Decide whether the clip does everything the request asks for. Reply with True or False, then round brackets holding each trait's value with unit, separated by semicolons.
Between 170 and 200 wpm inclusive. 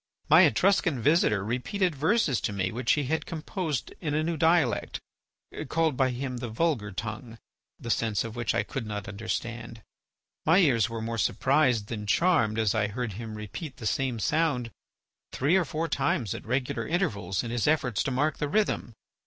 True (180 wpm)